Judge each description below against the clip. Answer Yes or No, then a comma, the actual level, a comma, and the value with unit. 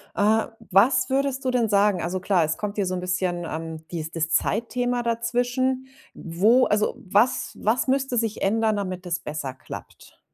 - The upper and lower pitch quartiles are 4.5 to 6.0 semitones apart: Yes, wide, 5.4 semitones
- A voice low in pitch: No, high, 210 Hz